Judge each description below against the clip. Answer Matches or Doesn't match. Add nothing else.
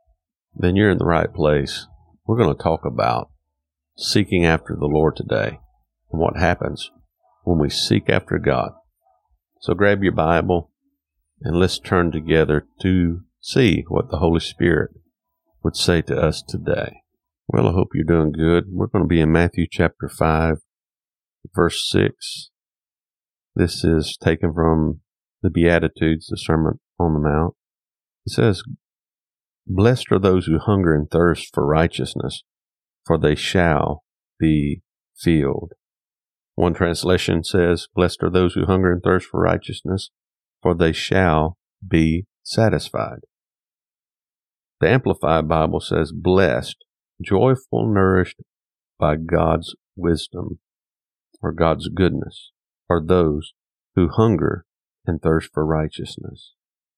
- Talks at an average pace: Doesn't match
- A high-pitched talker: Doesn't match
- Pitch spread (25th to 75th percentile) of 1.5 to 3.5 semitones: Matches